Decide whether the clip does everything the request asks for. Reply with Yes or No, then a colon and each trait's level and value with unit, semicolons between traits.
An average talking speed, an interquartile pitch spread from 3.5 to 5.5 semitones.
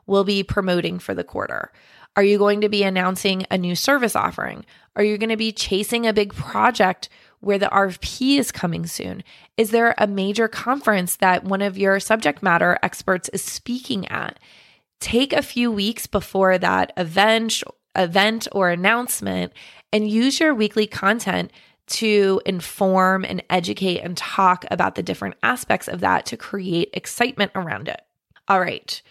No: average, 165 wpm; average, 2.9 semitones